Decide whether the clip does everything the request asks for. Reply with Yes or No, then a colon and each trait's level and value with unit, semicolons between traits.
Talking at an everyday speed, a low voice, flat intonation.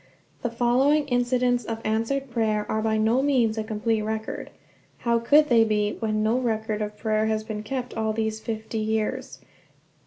No: average, 175 wpm; high, 220 Hz; narrow, 2.0 semitones